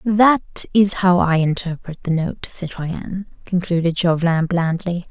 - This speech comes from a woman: Yes, female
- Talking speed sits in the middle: No, slow, 130 wpm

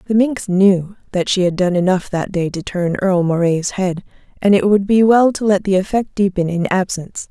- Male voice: No, female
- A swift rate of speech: Yes, fast, 220 wpm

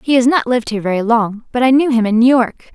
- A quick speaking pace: Yes, fast, 305 wpm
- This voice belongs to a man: No, female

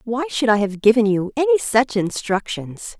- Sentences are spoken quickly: No, average, 180 wpm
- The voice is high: Yes, high, 215 Hz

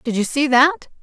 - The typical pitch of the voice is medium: No, very high, 255 Hz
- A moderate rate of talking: No, fast, 235 wpm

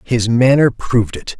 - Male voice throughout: Yes, male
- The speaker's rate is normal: Yes, average, 170 wpm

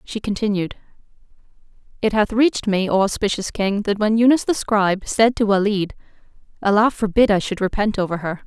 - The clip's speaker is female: Yes, female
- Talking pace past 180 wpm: No, average, 170 wpm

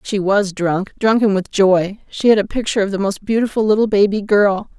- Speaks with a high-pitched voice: Yes, high, 200 Hz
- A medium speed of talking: No, fast, 215 wpm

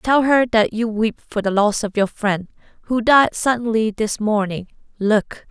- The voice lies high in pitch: Yes, high, 220 Hz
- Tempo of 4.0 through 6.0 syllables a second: Yes, 4.2 syllables/s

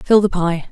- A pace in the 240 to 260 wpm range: Yes, fast, 250 wpm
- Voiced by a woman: Yes, female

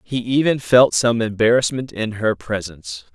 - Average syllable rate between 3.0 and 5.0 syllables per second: Yes, 4.7 syllables/s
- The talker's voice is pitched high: No, low, 115 Hz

